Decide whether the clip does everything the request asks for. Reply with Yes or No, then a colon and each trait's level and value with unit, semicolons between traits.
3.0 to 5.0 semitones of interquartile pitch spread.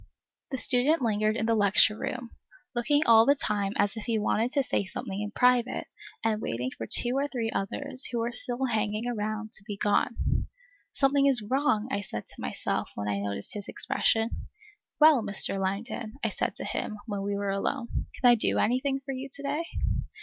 Yes: average, 3.9 semitones